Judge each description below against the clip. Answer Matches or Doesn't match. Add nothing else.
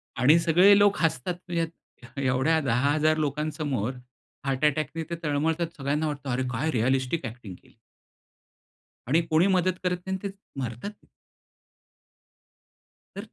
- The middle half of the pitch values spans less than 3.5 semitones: Doesn't match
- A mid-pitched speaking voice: Matches